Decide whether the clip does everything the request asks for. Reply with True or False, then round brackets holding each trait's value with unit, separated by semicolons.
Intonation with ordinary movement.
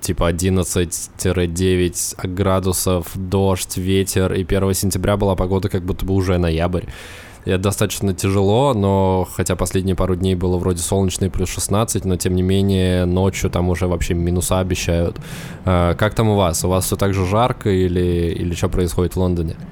False (1.4 semitones)